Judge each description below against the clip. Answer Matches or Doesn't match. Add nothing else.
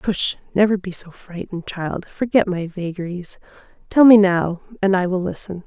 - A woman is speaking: Matches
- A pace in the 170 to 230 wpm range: Doesn't match